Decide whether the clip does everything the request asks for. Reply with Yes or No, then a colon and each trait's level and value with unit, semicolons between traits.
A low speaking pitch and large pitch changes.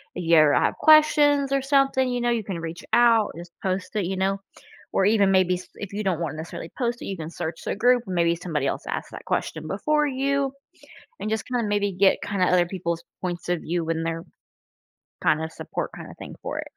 No: high, 190 Hz; wide, 6.0 semitones